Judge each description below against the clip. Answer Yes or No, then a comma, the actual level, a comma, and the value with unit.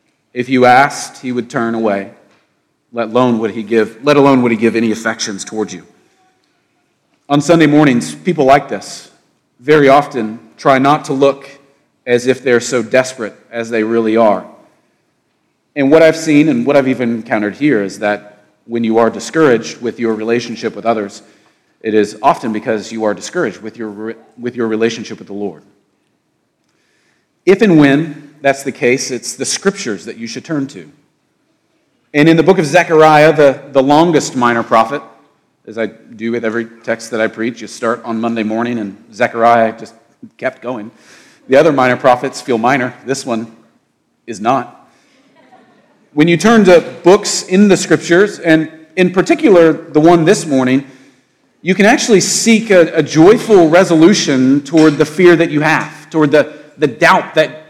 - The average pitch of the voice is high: No, low, 130 Hz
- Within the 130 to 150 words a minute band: No, average, 175 wpm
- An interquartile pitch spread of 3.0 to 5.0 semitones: No, wide, 5.6 semitones